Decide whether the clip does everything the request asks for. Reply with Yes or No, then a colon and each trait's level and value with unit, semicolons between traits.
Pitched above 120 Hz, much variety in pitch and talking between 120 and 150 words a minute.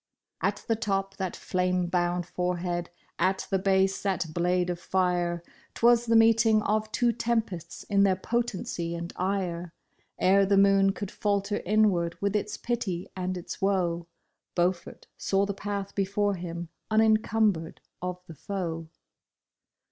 No: high, 190 Hz; average, 2.7 semitones; average, 145 wpm